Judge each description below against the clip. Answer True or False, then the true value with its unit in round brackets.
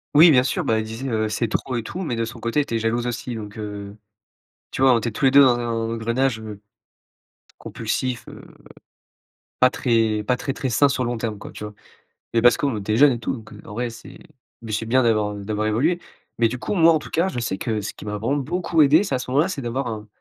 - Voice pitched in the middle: False (120 Hz)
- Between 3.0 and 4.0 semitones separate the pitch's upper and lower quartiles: True (3.5 semitones)